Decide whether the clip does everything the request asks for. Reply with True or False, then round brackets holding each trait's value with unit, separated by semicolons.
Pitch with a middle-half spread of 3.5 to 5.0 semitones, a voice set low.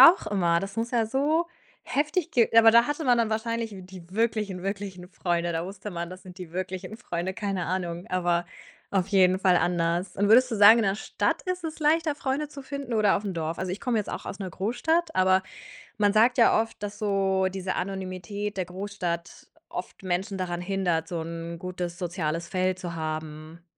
False (4.1 semitones; 190 Hz)